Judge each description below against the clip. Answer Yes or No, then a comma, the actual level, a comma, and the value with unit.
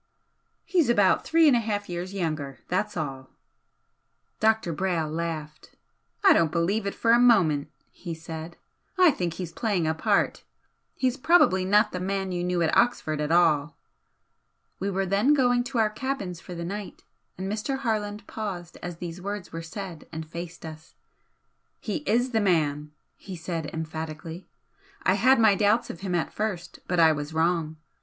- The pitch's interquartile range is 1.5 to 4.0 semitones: No, average, 4.6 semitones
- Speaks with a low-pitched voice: No, medium, 180 Hz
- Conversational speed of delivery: Yes, average, 170 wpm